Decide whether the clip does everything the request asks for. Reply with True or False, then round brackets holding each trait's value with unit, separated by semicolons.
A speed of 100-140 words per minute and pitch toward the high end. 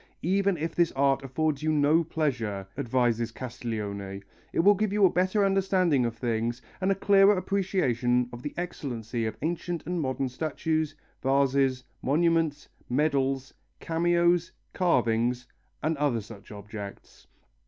False (135 wpm; 140 Hz)